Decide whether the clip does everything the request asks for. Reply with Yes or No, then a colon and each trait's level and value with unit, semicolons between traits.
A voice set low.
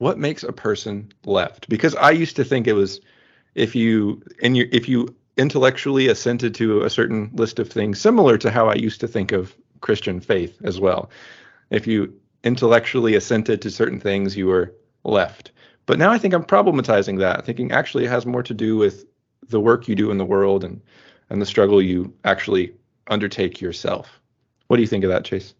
Yes: low, 115 Hz